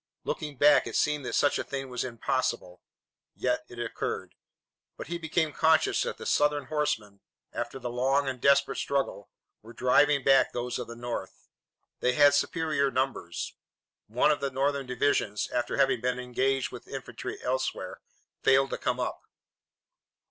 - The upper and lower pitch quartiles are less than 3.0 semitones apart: Yes, narrow, 2.6 semitones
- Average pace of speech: Yes, average, 160 wpm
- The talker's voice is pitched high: No, low, 135 Hz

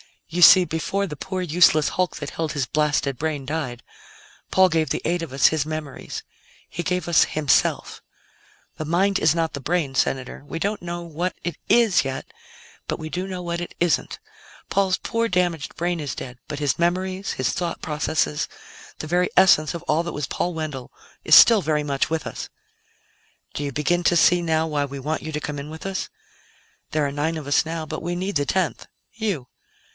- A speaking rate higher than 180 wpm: Yes, average, 200 wpm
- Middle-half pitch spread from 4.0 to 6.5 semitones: No, average, 3.2 semitones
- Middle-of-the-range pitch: Yes, medium, 160 Hz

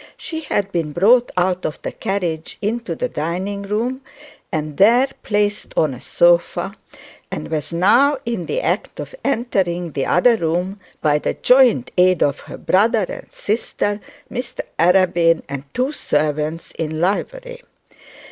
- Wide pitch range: Yes, wide, 5.8 semitones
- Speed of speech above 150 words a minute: No, average, 145 wpm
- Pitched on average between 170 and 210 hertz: Yes, medium, 185 Hz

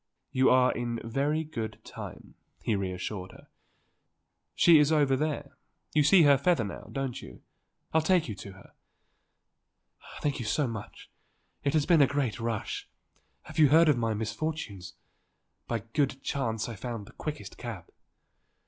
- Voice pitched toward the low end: Yes, low, 130 Hz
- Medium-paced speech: Yes, average, 155 wpm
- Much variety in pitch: No, average, 5.0 semitones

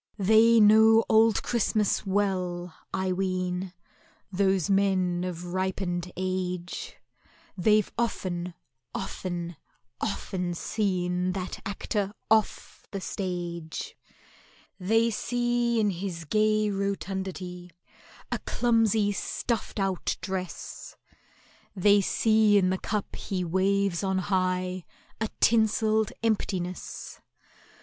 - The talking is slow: Yes, slow, 95 wpm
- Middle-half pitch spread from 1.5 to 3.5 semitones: Yes, average, 2.7 semitones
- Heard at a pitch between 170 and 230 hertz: Yes, high, 190 Hz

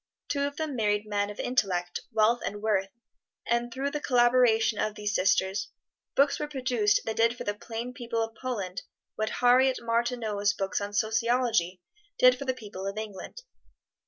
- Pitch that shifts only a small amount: No, average, 3.4 semitones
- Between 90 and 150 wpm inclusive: No, average, 170 wpm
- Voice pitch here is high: Yes, high, 225 Hz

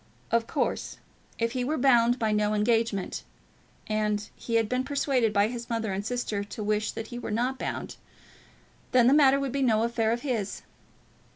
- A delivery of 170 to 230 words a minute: Yes, average, 185 wpm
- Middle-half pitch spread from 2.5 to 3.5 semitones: Yes, average, 2.9 semitones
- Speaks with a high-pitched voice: Yes, high, 230 Hz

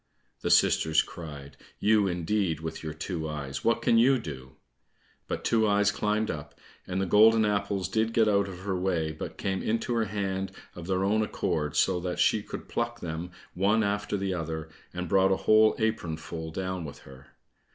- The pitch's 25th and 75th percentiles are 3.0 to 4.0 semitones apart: No, average, 4.6 semitones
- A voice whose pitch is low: Yes, very low, 95 Hz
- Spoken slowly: No, average, 185 wpm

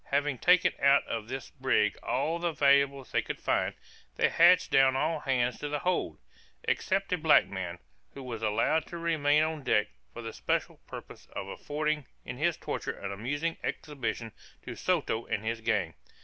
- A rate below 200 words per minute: Yes, average, 175 wpm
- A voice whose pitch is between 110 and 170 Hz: Yes, medium, 140 Hz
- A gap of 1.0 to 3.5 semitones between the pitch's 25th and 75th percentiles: No, average, 5.1 semitones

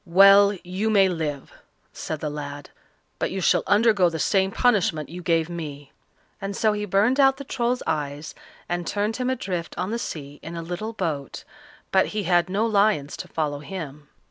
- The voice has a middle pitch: Yes, medium, 180 Hz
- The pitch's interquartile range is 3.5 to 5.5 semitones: Yes, average, 5.1 semitones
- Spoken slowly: No, average, 185 wpm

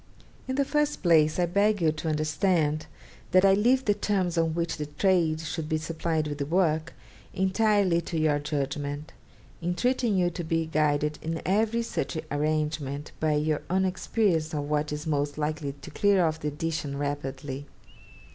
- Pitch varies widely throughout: No, average, 3.8 semitones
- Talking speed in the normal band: Yes, average, 170 wpm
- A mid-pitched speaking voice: Yes, medium, 160 Hz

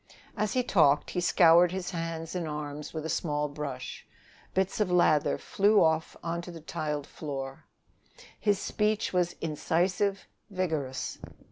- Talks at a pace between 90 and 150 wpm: Yes, average, 145 wpm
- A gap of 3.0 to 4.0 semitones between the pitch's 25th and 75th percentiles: Yes, average, 3.6 semitones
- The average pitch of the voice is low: No, medium, 165 Hz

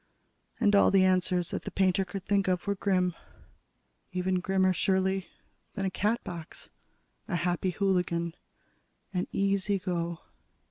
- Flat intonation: Yes, narrow, 1.5 semitones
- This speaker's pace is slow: Yes, slow, 130 wpm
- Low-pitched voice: No, medium, 185 Hz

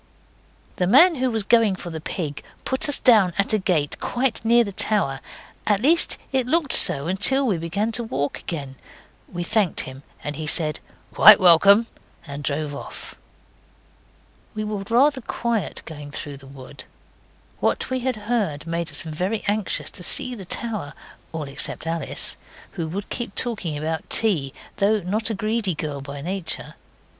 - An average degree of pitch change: No, wide, 6.6 semitones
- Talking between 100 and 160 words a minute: No, average, 170 wpm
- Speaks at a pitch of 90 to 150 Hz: No, high, 195 Hz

